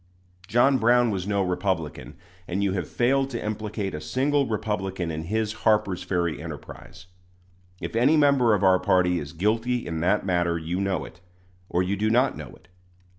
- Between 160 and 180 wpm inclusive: Yes, average, 175 wpm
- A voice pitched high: No, low, 100 Hz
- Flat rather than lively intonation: No, average, 4.3 semitones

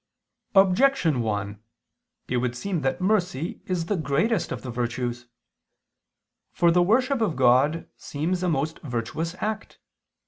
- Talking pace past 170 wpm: No, slow, 135 wpm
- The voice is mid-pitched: Yes, medium, 160 Hz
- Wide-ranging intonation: Yes, wide, 6.9 semitones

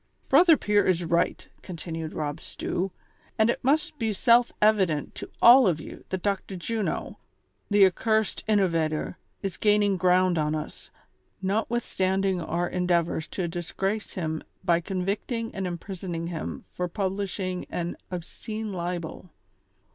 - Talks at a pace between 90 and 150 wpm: Yes, average, 140 wpm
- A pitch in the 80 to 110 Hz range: No, medium, 185 Hz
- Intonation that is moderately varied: Yes, average, 3.4 semitones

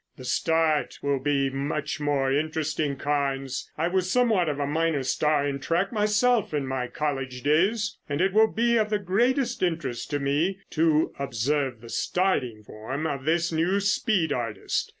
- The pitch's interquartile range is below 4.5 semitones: No, average, 5.1 semitones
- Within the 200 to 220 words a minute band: No, average, 170 wpm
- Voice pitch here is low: No, medium, 150 Hz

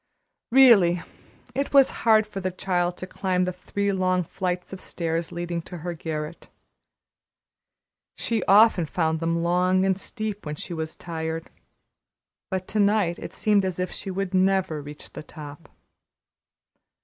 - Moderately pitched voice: Yes, medium, 180 Hz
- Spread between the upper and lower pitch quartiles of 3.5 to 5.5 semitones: No, average, 2.7 semitones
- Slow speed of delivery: No, average, 150 wpm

